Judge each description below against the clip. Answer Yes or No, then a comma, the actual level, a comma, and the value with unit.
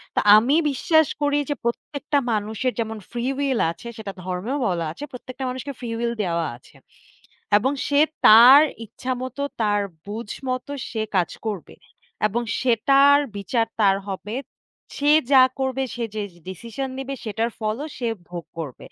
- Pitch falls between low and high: No, high, 235 Hz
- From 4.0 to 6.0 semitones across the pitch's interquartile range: Yes, average, 4.3 semitones